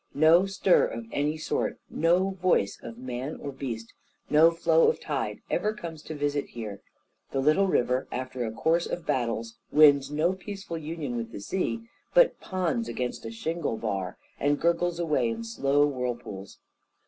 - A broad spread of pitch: Yes, wide, 5.8 semitones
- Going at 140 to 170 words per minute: Yes, average, 165 wpm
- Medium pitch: Yes, medium, 145 Hz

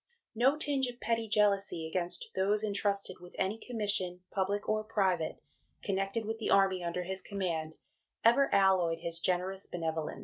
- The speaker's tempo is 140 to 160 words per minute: Yes, average, 150 wpm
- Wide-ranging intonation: No, average, 3.2 semitones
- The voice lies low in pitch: No, high, 195 Hz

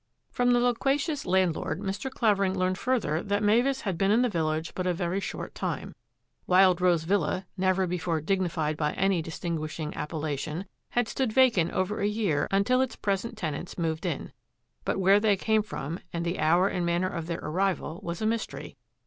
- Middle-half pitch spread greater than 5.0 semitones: No, average, 4.0 semitones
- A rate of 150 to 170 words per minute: No, average, 185 wpm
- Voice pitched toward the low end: No, medium, 185 Hz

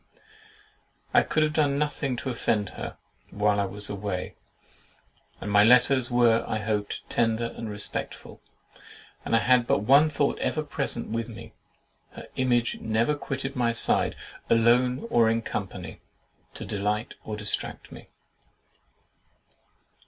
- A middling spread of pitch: Yes, average, 3.6 semitones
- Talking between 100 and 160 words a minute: Yes, average, 140 wpm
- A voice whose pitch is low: Yes, low, 115 Hz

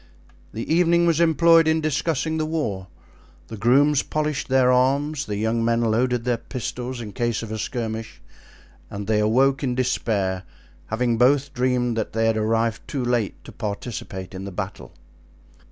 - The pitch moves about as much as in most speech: Yes, average, 4.1 semitones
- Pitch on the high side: No, low, 120 Hz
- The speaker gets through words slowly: No, average, 165 wpm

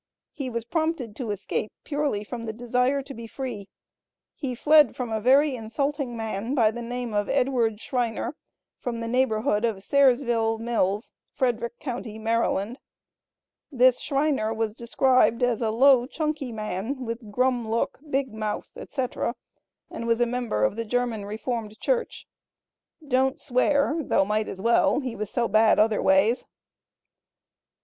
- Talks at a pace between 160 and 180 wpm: No, average, 150 wpm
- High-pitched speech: Yes, high, 235 Hz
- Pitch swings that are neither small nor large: Yes, average, 3.1 semitones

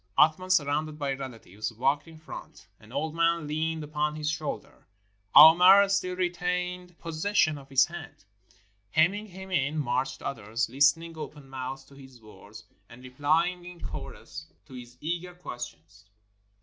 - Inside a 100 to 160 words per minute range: Yes, average, 150 wpm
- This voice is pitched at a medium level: Yes, medium, 150 Hz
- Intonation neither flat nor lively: Yes, average, 4.6 semitones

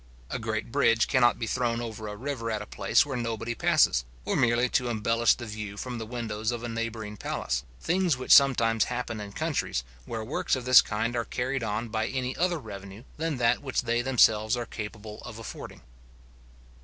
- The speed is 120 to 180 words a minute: No, average, 195 wpm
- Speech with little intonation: Yes, narrow, 2.3 semitones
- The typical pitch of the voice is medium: No, low, 115 Hz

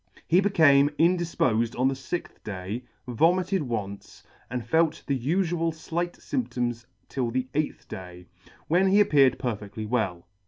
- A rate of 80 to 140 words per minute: Yes, slow, 135 wpm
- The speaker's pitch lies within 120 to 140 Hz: Yes, low, 135 Hz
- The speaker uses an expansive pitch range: Yes, wide, 6.6 semitones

